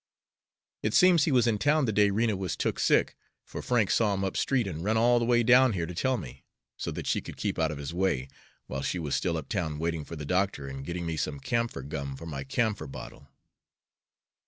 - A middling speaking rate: No, fast, 235 wpm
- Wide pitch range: Yes, wide, 7.2 semitones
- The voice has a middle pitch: No, very low, 95 Hz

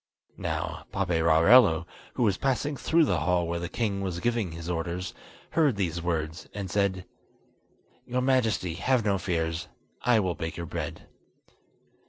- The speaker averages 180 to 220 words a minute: No, average, 150 wpm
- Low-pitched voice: Yes, very low, 90 Hz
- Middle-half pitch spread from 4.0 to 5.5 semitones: Yes, average, 5.2 semitones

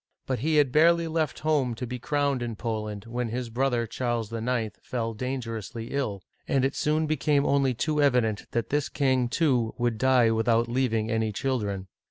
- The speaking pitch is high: No, low, 125 Hz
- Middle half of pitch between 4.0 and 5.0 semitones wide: No, average, 3.5 semitones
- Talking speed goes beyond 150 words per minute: Yes, average, 180 wpm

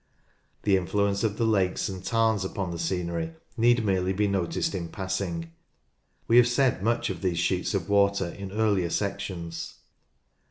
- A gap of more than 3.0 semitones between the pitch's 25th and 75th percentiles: No, average, 2.7 semitones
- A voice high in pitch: No, very low, 95 Hz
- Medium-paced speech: Yes, average, 160 wpm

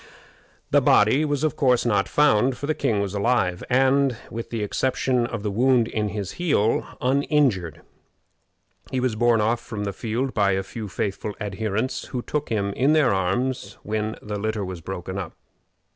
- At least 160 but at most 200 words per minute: Yes, average, 175 wpm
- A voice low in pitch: Yes, low, 110 Hz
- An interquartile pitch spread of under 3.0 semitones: No, average, 4.3 semitones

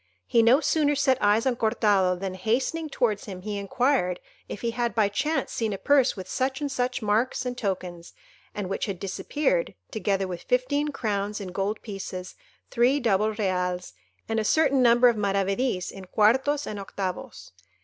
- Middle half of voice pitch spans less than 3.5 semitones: No, average, 4.8 semitones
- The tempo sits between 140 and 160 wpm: No, average, 175 wpm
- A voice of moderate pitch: No, high, 220 Hz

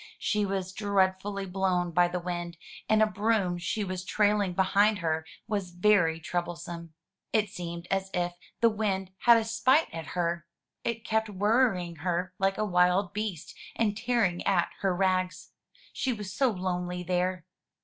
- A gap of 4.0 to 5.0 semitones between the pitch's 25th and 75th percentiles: No, average, 3.0 semitones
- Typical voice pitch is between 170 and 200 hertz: Yes, high, 190 Hz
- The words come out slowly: No, average, 160 wpm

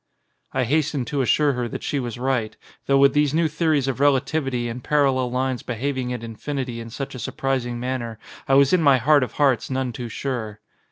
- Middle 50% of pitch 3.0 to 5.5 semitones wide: No, narrow, 2.5 semitones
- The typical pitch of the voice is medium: No, low, 130 Hz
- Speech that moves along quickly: Yes, fast, 210 wpm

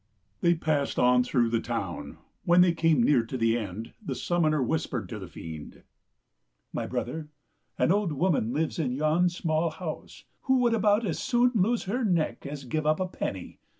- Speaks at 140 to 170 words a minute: No, average, 185 wpm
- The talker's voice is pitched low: No, medium, 155 Hz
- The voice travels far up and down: Yes, wide, 6.6 semitones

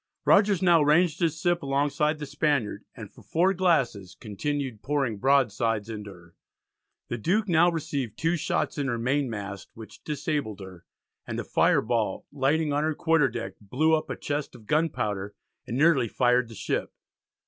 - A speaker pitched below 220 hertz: Yes, medium, 140 Hz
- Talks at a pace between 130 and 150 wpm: No, average, 170 wpm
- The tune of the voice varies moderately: No, wide, 6.0 semitones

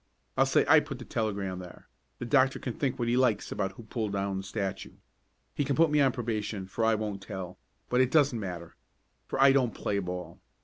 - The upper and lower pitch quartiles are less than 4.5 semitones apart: No, average, 5.1 semitones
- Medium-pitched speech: No, low, 110 Hz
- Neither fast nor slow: No, fast, 220 wpm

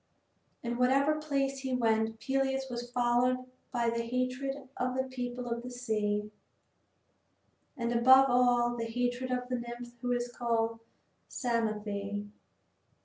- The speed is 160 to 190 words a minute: No, average, 140 wpm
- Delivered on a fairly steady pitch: Yes, narrow, 1.4 semitones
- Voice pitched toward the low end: No, high, 245 Hz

